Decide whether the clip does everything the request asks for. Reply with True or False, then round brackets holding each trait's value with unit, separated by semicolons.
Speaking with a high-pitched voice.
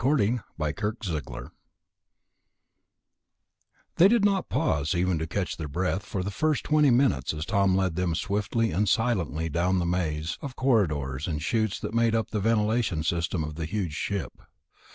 False (95 Hz)